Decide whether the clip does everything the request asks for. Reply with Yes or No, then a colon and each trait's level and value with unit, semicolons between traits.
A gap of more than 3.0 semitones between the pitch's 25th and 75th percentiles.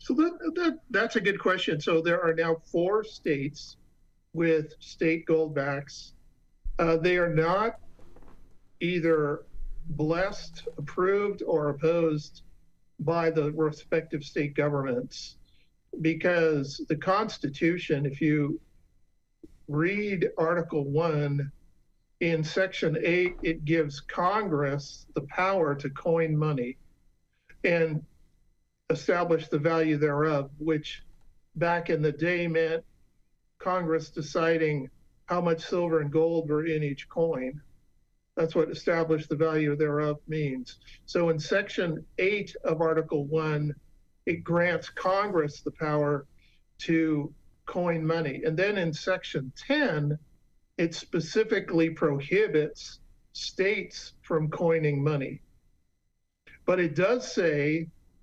No: narrow, 2.6 semitones